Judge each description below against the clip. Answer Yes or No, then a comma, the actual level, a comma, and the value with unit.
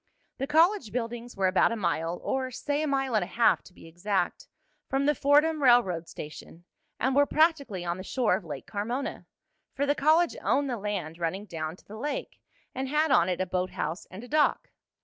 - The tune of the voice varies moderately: No, wide, 7.5 semitones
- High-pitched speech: Yes, high, 235 Hz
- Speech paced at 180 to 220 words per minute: Yes, fast, 205 wpm